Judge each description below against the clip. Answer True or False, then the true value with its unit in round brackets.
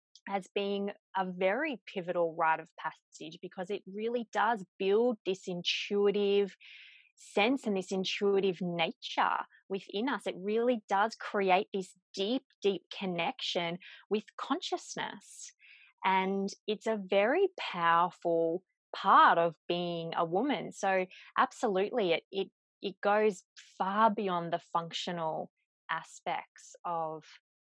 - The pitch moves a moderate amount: True (3.2 semitones)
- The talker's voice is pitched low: False (195 Hz)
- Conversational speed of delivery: False (115 wpm)